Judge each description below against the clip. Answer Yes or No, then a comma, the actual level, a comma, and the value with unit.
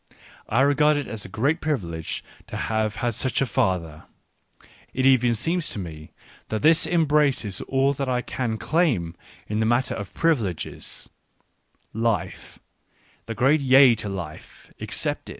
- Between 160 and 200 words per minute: No, average, 150 wpm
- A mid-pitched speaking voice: No, low, 120 Hz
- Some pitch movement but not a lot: No, wide, 5.7 semitones